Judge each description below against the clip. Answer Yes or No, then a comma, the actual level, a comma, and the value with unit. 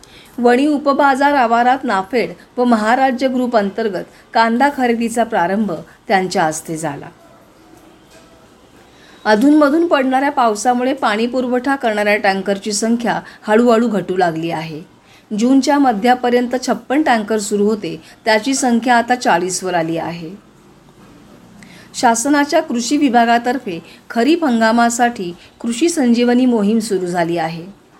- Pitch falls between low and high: No, high, 235 Hz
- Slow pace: No, average, 105 wpm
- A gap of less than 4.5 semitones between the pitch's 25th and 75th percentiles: Yes, average, 3.9 semitones